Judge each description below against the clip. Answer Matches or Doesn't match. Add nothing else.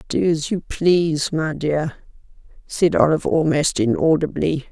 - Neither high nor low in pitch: Matches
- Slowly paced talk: Matches